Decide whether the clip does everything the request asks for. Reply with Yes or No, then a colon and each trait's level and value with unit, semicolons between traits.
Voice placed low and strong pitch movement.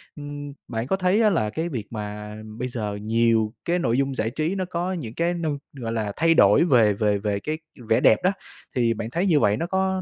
Yes: low, 125 Hz; wide, 7.7 semitones